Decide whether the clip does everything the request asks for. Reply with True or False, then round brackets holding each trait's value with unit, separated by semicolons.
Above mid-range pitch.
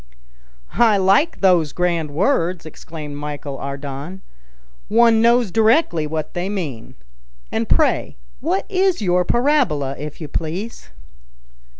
False (180 Hz)